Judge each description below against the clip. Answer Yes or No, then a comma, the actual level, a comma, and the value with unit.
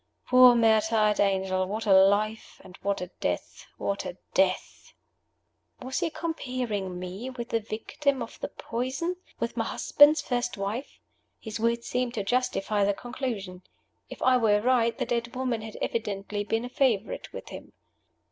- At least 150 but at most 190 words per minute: Yes, average, 160 wpm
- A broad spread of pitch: No, average, 3.9 semitones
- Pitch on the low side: No, high, 225 Hz